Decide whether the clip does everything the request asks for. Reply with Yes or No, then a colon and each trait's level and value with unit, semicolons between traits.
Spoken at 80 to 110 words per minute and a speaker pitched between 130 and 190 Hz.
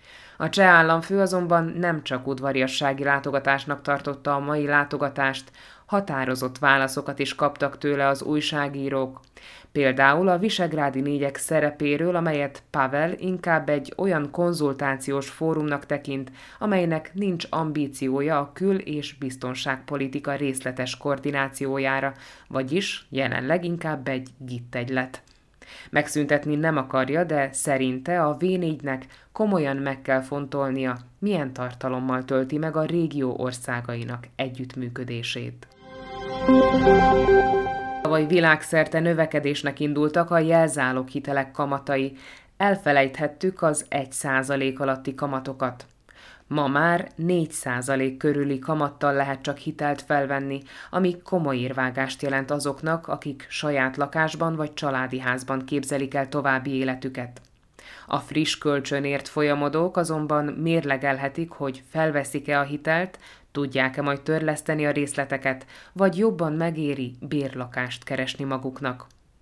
Yes: slow, 105 wpm; medium, 140 Hz